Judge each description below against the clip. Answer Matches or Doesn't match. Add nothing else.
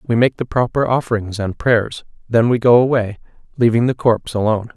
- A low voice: Matches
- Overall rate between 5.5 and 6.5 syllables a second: Matches